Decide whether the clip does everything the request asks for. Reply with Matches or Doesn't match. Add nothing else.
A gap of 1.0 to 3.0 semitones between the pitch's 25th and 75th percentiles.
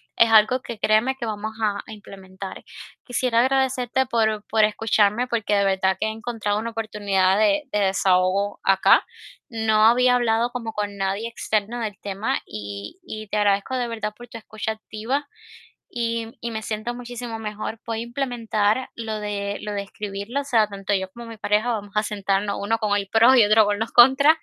Matches